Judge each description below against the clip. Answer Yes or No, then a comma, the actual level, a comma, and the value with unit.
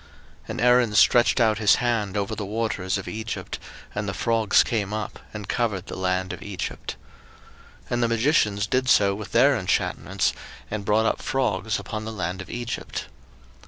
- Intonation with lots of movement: No, average, 2.8 semitones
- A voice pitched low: Yes, low, 105 Hz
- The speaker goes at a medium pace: Yes, average, 180 wpm